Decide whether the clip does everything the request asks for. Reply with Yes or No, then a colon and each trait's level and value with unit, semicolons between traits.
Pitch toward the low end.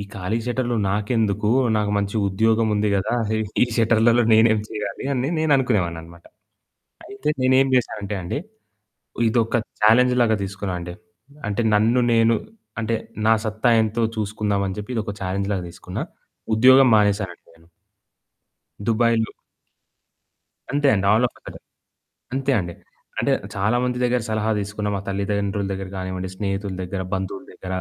Yes: low, 105 Hz